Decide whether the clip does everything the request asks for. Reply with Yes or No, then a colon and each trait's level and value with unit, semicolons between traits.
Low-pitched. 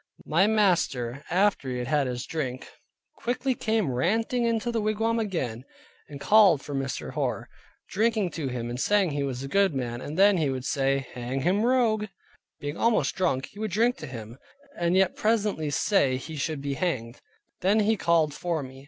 No: medium, 165 Hz